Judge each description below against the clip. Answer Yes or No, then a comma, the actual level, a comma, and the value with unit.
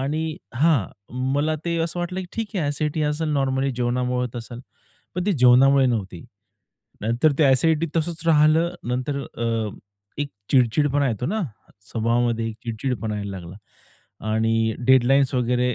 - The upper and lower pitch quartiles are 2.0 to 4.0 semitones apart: No, average, 4.6 semitones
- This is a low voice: Yes, low, 130 Hz